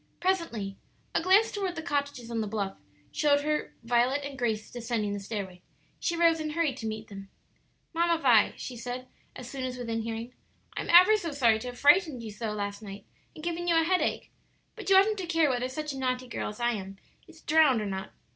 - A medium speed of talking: No, fast, 220 wpm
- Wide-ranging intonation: Yes, wide, 6.6 semitones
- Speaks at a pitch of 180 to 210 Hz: No, very high, 255 Hz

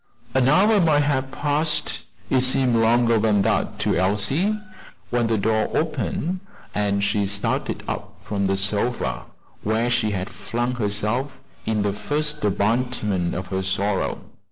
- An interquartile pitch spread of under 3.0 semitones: No, average, 4.6 semitones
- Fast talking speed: No, average, 145 wpm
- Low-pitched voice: Yes, low, 115 Hz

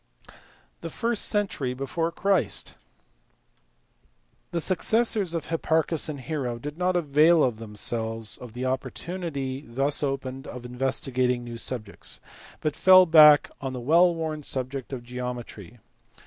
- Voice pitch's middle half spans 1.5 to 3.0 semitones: No, average, 4.9 semitones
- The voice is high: No, low, 135 Hz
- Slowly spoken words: Yes, slow, 130 wpm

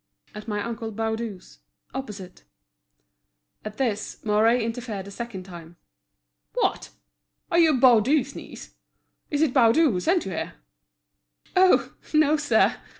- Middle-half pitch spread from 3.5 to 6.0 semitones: Yes, average, 4.8 semitones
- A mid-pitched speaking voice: No, high, 230 Hz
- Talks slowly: Yes, slow, 125 wpm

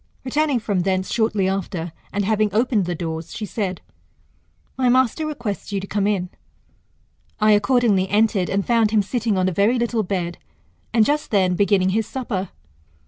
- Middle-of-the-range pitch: No, high, 205 Hz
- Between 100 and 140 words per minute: No, average, 170 wpm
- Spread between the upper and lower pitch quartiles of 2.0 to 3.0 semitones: No, average, 3.6 semitones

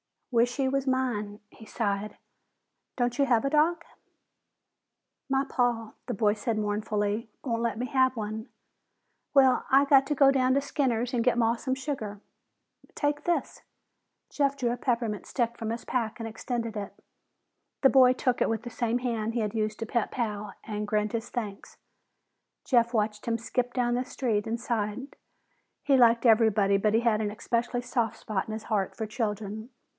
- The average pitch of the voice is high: Yes, high, 235 Hz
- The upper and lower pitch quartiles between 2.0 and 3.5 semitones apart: Yes, average, 2.9 semitones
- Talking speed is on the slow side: No, average, 180 wpm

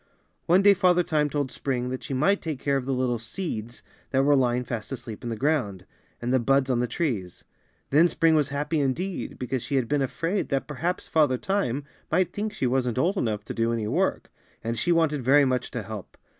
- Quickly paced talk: Yes, fast, 220 wpm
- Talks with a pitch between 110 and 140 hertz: Yes, low, 135 Hz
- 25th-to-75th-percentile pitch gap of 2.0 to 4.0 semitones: No, average, 4.6 semitones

